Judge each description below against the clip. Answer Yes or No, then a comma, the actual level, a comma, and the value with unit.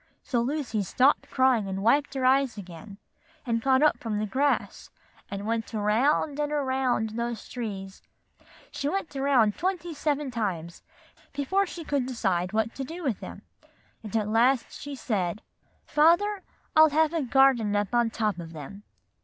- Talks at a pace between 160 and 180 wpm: Yes, average, 170 wpm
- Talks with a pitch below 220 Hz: No, high, 245 Hz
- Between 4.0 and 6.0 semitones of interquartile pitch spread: Yes, average, 5.2 semitones